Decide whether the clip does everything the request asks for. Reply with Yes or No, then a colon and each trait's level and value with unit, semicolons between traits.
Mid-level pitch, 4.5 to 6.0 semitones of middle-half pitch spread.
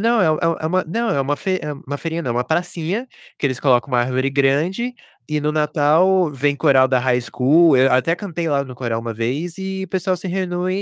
Yes: medium, 155 Hz; average, 5.2 semitones